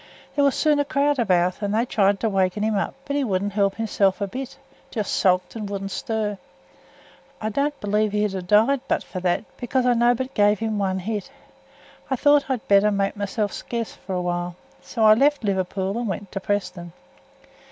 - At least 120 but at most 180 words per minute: No, fast, 205 wpm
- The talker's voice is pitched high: Yes, high, 210 Hz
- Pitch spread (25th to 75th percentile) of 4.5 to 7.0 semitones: No, average, 3.5 semitones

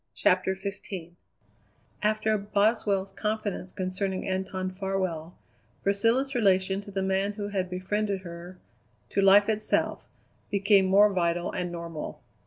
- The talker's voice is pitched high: Yes, high, 195 Hz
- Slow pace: Yes, slow, 120 wpm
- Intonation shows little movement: Yes, narrow, 1.7 semitones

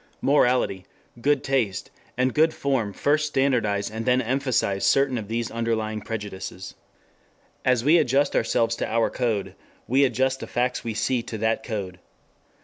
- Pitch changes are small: No, average, 3.5 semitones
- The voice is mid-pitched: No, low, 120 Hz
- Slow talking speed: No, average, 150 wpm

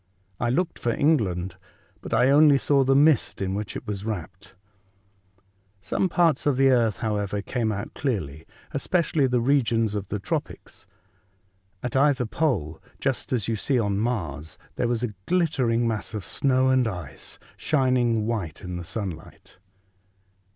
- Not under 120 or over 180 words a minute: Yes, average, 155 wpm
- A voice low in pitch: Yes, low, 115 Hz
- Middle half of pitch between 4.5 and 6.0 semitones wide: Yes, average, 5.0 semitones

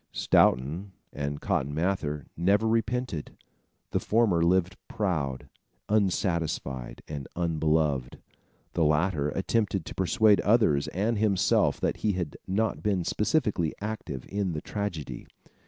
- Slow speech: Yes, slow, 120 wpm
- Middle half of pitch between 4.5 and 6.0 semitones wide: Yes, wide, 5.4 semitones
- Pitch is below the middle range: Yes, very low, 90 Hz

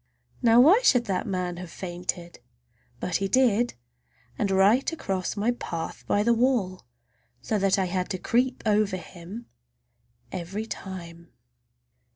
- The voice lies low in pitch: No, high, 195 Hz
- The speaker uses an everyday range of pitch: Yes, average, 4.3 semitones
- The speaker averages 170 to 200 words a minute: No, average, 140 wpm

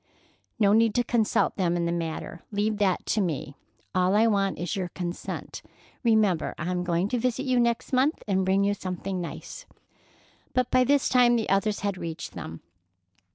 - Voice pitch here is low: No, high, 200 Hz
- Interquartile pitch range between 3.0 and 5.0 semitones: Yes, average, 4.4 semitones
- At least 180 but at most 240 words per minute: Yes, average, 185 wpm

